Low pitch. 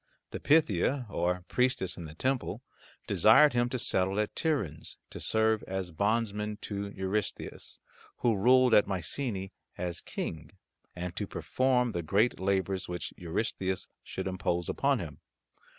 Yes: low, 100 Hz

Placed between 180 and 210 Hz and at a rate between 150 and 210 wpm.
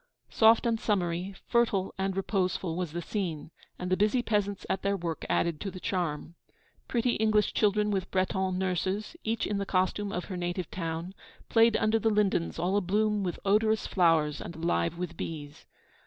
Yes: high, 190 Hz; average, 175 wpm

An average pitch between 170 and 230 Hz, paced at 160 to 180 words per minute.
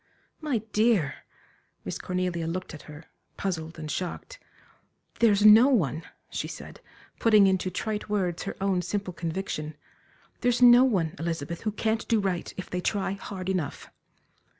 No: high, 190 Hz; average, 150 wpm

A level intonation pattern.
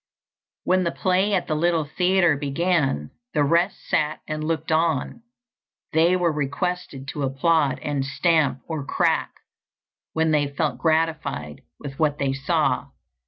No: average, 3.2 semitones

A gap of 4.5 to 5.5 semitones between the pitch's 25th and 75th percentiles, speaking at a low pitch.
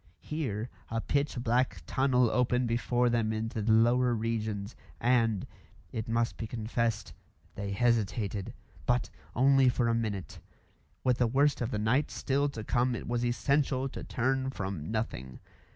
No: narrow, 2.5 semitones; low, 120 Hz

